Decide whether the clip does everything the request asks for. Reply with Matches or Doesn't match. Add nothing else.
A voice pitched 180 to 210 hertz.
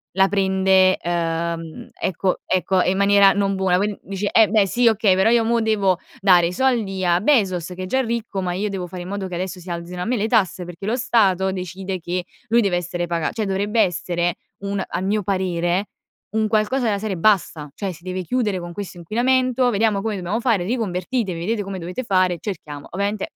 Matches